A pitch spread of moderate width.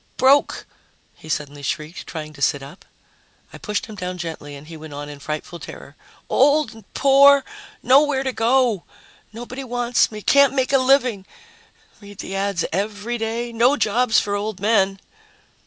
No: wide, 6.9 semitones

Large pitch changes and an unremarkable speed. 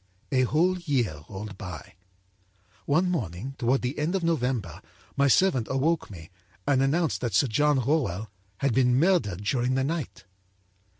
Yes: wide, 5.8 semitones; average, 155 wpm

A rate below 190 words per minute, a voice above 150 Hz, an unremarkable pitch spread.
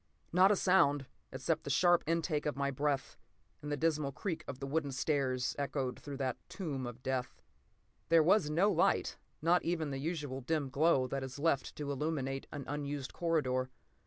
No: average, 180 wpm; medium, 145 Hz; average, 3.4 semitones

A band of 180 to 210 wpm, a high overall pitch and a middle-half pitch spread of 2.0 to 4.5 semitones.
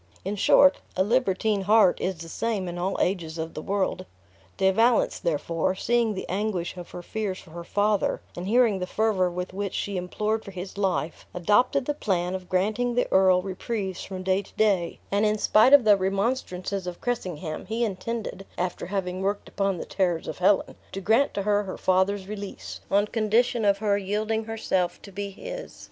Yes: average, 190 wpm; high, 195 Hz; average, 2.8 semitones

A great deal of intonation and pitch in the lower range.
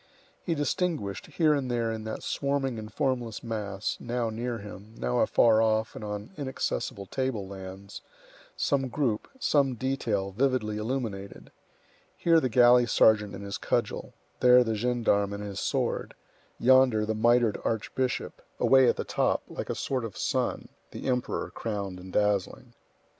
No: average, 3.9 semitones; low, 115 Hz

